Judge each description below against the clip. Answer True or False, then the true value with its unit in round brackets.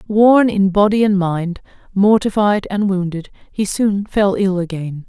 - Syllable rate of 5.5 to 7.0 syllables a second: False (4.1 syllables/s)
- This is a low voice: False (195 Hz)